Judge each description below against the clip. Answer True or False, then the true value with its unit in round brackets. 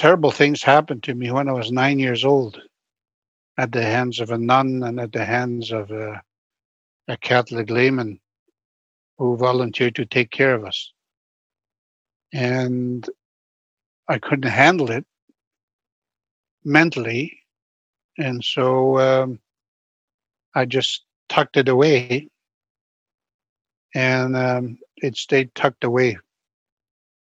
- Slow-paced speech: True (115 wpm)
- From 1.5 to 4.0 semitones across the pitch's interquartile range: True (2.7 semitones)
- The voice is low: True (125 Hz)